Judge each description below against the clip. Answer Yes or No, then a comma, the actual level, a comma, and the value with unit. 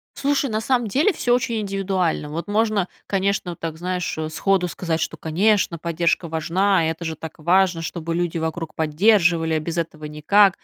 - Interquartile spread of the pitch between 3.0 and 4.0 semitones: Yes, average, 3.7 semitones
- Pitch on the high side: No, medium, 175 Hz